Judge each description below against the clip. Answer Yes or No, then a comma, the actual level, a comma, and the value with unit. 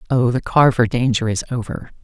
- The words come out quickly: No, average, 175 wpm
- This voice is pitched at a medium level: No, low, 120 Hz